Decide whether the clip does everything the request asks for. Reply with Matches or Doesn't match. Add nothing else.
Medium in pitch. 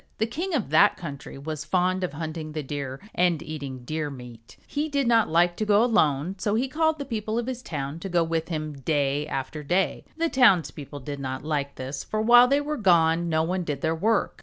Matches